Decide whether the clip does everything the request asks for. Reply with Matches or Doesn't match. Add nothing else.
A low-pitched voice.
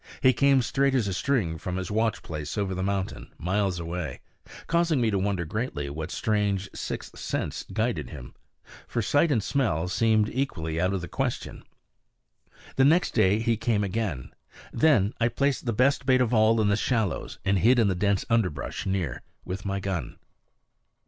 Matches